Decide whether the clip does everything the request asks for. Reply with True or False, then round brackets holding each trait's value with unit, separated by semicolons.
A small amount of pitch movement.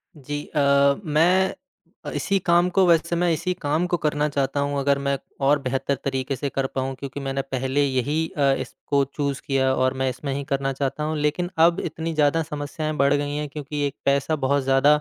True (2.1 semitones)